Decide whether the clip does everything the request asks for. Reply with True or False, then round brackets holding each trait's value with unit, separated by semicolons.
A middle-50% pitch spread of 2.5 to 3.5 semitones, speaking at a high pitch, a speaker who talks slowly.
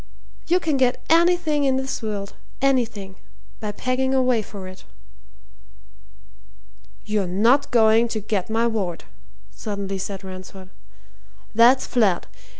False (4.9 semitones; 225 Hz; 120 wpm)